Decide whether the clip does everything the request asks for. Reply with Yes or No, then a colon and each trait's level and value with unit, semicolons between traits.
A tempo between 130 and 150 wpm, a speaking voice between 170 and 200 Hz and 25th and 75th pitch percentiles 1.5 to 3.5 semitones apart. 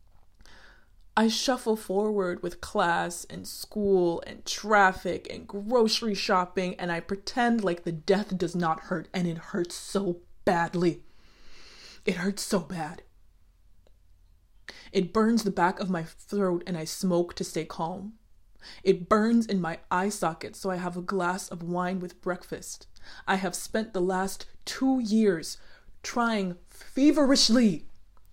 Yes: average, 140 wpm; medium, 185 Hz; average, 3.2 semitones